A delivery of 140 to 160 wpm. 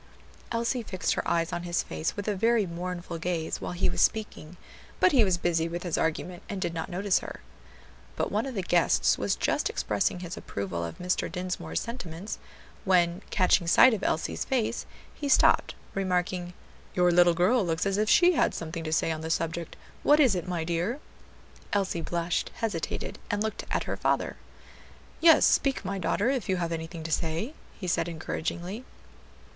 No: average, 185 wpm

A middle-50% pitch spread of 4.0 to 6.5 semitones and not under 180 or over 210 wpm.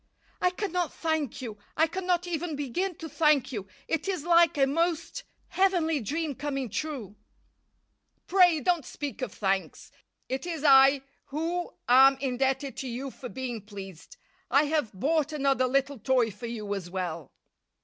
No: average, 4.8 semitones; average, 155 wpm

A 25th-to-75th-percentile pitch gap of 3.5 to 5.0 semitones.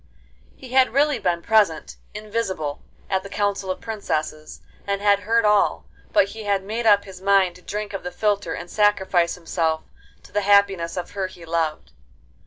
No: average, 2.9 semitones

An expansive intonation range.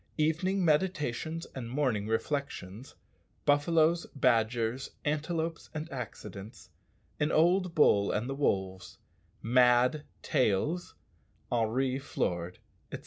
Yes: wide, 5.8 semitones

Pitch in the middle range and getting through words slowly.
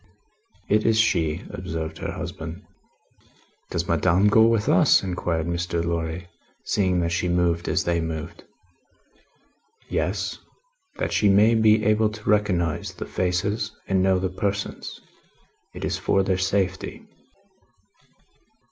No: very low, 90 Hz; slow, 130 wpm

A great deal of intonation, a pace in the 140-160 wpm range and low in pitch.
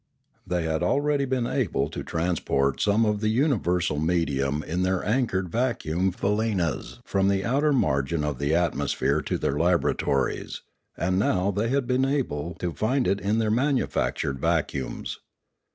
Yes: wide, 6.4 semitones; average, 155 wpm; very low, 95 Hz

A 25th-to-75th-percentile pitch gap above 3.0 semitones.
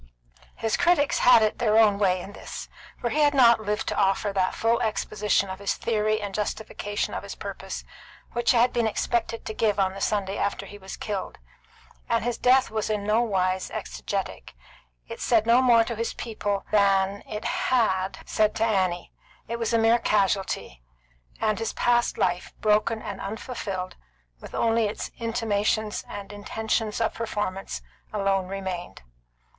No: narrow, 2.6 semitones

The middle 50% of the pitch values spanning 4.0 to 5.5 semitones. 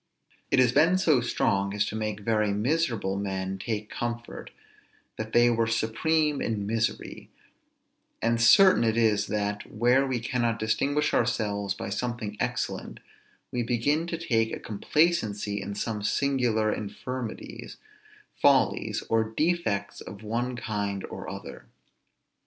No: average, 3.2 semitones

